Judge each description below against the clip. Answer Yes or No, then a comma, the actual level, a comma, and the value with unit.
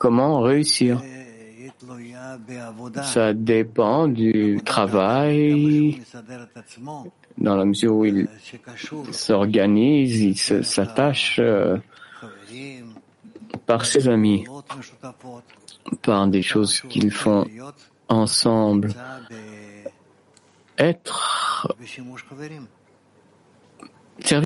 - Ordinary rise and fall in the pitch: Yes, average, 3.7 semitones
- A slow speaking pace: Yes, slow, 60 wpm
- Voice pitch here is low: Yes, low, 120 Hz